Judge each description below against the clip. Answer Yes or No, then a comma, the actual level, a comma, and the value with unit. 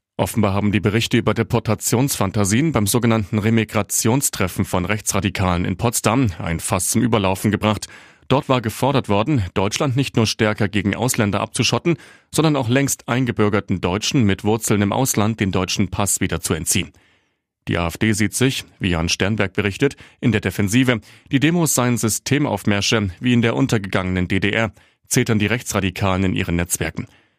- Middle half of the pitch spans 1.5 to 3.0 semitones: No, average, 3.4 semitones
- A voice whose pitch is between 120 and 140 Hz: No, low, 110 Hz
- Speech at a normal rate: Yes, average, 155 wpm